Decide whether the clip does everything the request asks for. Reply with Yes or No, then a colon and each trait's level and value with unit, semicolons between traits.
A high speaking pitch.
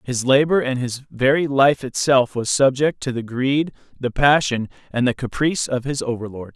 No: low, 130 Hz